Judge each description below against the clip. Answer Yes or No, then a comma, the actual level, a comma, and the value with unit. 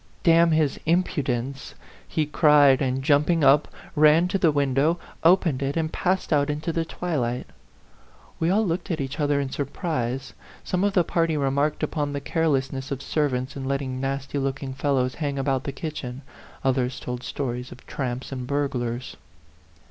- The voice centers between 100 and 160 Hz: Yes, medium, 140 Hz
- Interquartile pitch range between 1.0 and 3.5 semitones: Yes, average, 3.1 semitones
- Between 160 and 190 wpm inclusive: Yes, average, 170 wpm